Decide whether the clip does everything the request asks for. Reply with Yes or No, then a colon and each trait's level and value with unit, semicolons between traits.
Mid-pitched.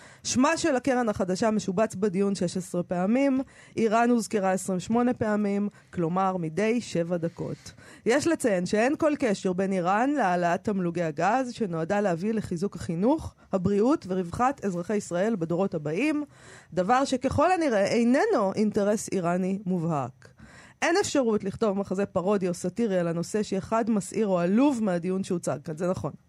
No: high, 200 Hz